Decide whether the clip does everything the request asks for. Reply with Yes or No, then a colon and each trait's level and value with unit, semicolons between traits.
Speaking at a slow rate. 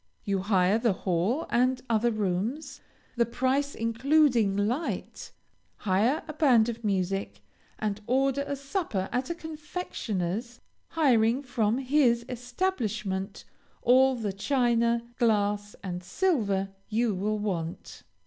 Yes: slow, 120 wpm